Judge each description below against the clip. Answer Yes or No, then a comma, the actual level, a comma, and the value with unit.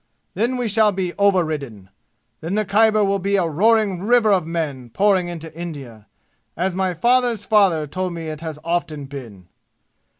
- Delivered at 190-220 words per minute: No, average, 165 wpm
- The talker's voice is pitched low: No, medium, 180 Hz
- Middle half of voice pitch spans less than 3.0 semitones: No, average, 4.8 semitones